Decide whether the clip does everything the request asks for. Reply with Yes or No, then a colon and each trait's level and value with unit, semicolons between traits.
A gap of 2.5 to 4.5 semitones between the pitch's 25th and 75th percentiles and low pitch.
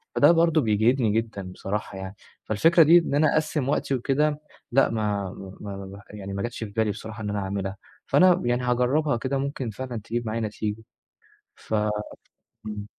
No: average, 5.0 semitones; low, 115 Hz